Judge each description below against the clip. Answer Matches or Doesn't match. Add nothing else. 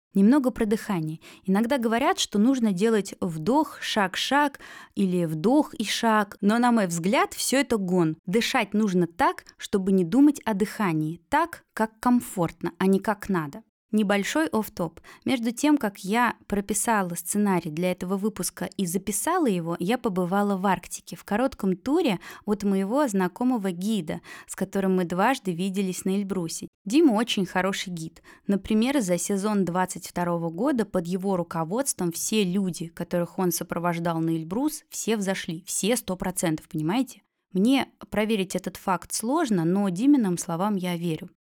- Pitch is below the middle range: Doesn't match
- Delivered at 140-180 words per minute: Matches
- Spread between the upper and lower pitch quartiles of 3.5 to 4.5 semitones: Matches